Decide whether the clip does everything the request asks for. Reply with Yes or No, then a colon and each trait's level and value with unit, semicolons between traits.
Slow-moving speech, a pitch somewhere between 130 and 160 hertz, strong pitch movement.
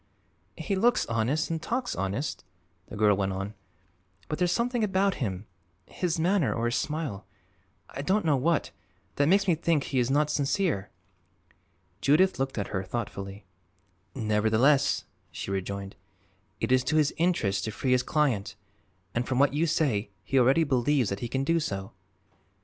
No: average, 165 wpm; low, 135 Hz; wide, 7.3 semitones